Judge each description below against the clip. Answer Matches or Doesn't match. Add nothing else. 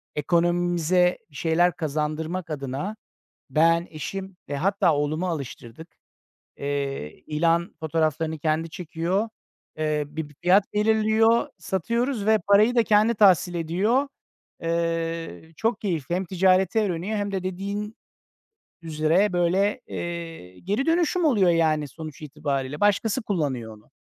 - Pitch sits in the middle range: Matches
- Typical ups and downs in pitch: Matches